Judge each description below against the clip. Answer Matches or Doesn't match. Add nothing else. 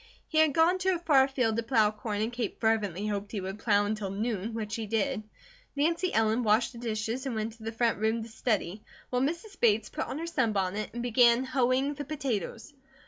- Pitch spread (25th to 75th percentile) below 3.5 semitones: Doesn't match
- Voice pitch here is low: Doesn't match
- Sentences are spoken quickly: Matches